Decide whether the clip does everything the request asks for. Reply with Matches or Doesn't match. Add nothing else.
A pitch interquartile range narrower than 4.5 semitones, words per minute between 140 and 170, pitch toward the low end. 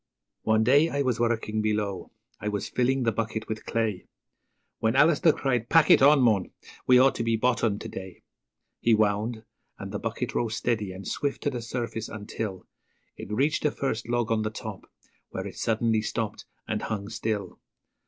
Doesn't match